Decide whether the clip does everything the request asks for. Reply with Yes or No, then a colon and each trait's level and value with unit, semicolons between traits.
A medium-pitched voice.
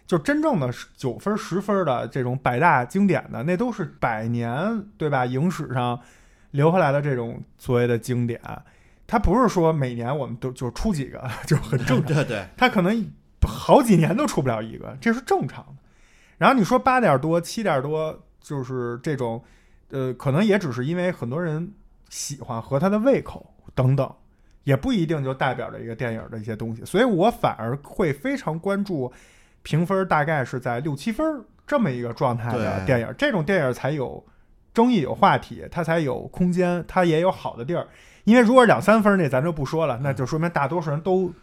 Yes: medium, 150 Hz